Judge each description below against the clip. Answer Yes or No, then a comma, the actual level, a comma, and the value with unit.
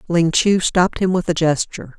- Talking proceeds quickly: Yes, fast, 210 wpm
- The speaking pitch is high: No, medium, 170 Hz